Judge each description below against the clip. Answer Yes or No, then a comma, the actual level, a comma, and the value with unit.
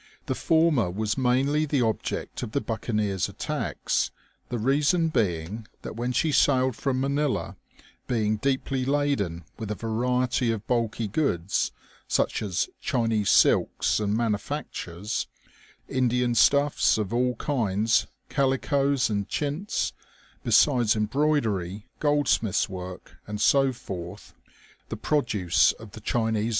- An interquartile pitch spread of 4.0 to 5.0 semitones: Yes, average, 4.7 semitones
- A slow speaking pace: Yes, slow, 130 wpm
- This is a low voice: Yes, low, 120 Hz